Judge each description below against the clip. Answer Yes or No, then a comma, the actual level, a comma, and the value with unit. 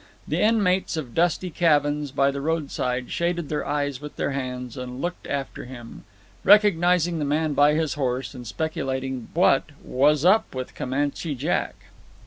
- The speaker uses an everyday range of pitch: Yes, average, 4.0 semitones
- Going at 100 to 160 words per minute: Yes, average, 155 wpm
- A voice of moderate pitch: Yes, medium, 145 Hz